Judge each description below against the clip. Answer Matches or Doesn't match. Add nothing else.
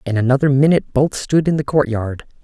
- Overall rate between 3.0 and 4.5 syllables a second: Doesn't match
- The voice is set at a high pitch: Doesn't match